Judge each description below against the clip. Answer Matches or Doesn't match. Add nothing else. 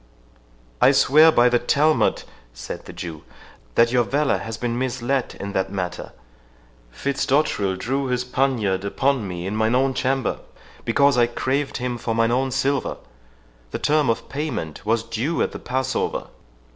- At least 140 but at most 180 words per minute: Matches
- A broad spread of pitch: Doesn't match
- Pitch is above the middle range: Doesn't match